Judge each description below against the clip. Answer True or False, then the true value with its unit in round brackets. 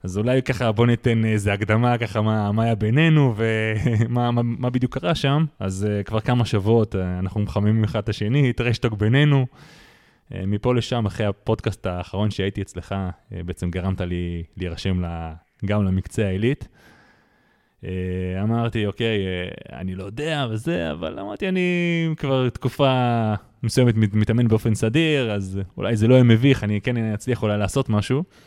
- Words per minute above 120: True (150 wpm)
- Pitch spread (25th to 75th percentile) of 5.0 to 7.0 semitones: False (3.9 semitones)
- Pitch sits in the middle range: False (110 Hz)